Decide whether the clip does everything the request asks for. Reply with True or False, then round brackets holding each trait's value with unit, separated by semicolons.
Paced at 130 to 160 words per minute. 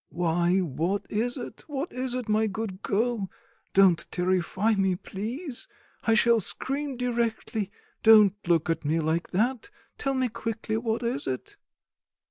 True (145 wpm)